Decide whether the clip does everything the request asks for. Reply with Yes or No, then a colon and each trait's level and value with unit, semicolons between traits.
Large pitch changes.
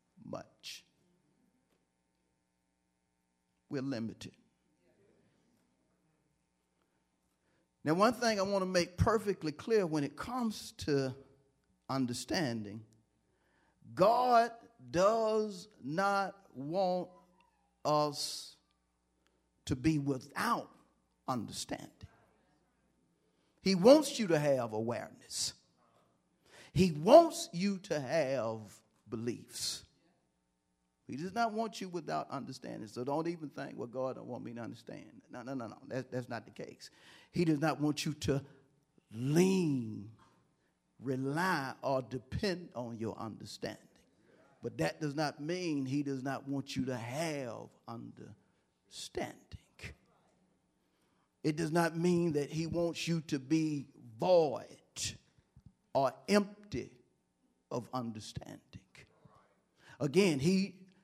Yes: wide, 8.3 semitones